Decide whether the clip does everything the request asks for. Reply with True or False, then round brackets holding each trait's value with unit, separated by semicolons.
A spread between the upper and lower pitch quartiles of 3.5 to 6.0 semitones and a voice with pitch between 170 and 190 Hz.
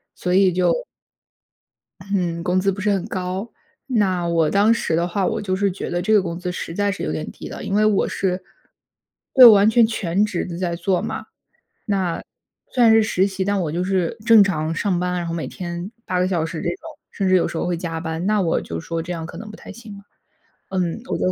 False (2.8 semitones; 185 Hz)